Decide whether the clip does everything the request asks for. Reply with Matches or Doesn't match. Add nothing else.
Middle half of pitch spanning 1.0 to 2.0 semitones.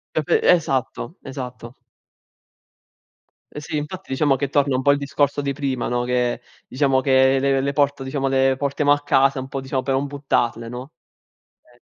Matches